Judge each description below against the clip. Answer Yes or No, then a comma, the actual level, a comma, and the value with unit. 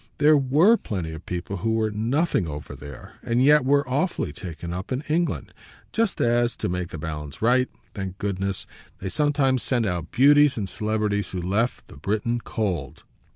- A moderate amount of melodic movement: No, wide, 6.6 semitones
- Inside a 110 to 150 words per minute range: No, average, 175 wpm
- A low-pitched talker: Yes, low, 110 Hz